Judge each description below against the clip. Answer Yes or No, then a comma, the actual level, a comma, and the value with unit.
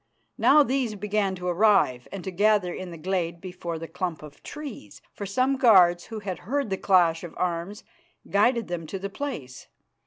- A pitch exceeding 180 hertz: Yes, high, 190 Hz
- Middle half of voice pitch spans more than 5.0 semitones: No, average, 3.7 semitones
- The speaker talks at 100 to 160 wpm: No, average, 185 wpm